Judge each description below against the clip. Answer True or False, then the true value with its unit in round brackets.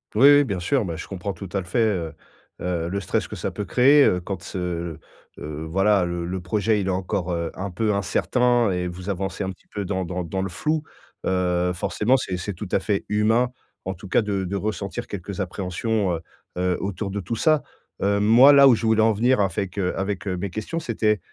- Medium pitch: False (100 Hz)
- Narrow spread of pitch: False (3.2 semitones)